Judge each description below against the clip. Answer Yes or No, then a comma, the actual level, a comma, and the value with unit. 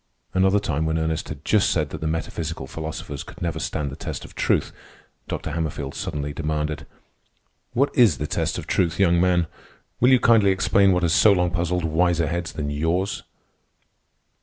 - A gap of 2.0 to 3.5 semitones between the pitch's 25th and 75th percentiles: Yes, average, 3.0 semitones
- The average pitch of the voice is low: Yes, very low, 85 Hz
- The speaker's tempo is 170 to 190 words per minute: Yes, average, 180 wpm